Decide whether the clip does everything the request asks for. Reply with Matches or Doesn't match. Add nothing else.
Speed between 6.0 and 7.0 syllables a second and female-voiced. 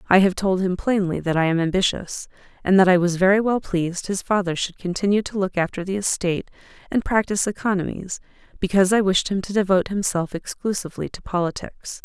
Matches